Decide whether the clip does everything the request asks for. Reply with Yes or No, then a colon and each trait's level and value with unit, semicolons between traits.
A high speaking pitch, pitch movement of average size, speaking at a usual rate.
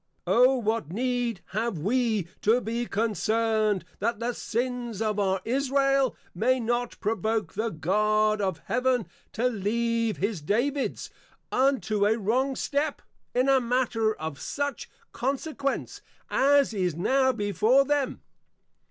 No: high, 230 Hz; average, 3.4 semitones; slow, 130 wpm